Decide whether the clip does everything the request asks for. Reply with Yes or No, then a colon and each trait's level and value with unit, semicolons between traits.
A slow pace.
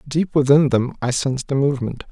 No: average, 200 wpm